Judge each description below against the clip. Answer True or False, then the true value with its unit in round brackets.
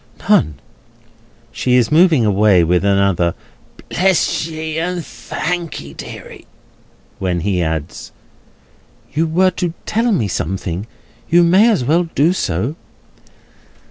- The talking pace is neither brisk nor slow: False (115 wpm)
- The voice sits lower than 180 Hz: True (140 Hz)